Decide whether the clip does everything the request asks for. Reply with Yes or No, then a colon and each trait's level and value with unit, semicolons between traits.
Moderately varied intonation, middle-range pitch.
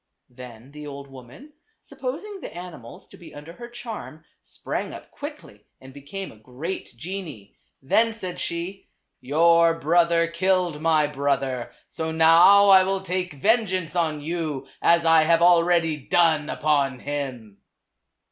Yes: average, 4.2 semitones; medium, 165 Hz